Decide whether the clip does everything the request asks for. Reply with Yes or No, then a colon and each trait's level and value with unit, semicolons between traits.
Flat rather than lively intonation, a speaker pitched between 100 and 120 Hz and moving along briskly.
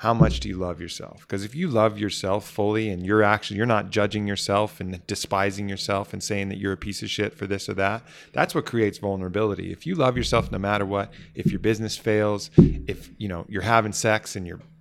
Yes: narrow, 1.7 semitones; low, 105 Hz; fast, 230 wpm